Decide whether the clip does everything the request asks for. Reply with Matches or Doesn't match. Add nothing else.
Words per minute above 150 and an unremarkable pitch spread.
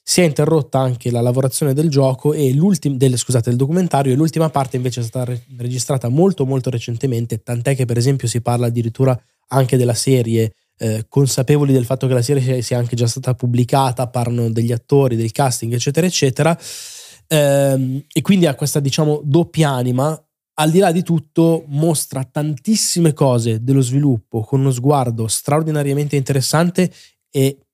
Matches